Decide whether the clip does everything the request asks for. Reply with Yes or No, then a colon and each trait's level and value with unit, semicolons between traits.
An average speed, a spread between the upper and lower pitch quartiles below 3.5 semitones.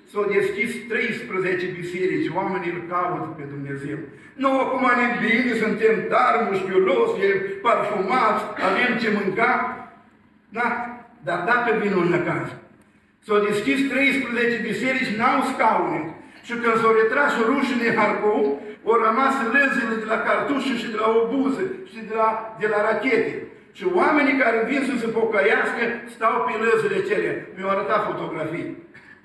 Yes: average, 150 wpm; average, 3.0 semitones